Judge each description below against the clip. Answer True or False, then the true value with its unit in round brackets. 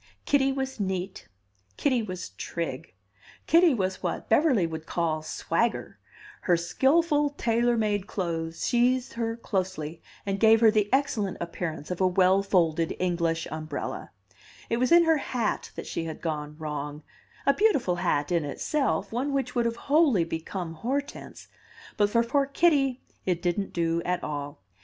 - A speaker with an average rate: True (155 wpm)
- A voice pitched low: False (195 Hz)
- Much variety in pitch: True (7.2 semitones)